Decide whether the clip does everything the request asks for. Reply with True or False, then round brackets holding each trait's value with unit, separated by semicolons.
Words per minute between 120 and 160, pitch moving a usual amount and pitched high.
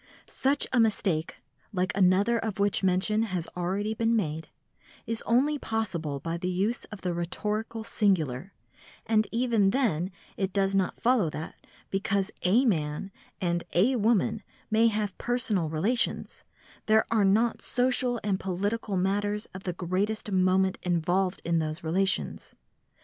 True (145 wpm; 3.6 semitones; 195 Hz)